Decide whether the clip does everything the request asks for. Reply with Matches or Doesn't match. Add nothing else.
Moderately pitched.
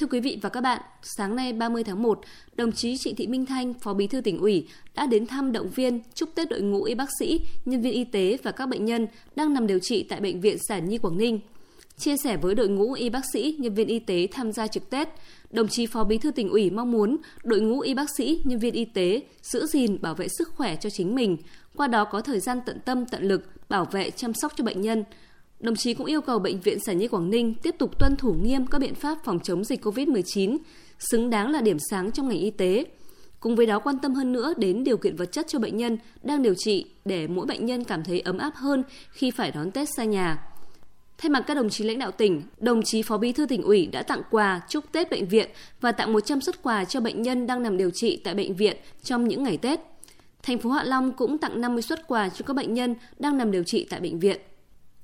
Doesn't match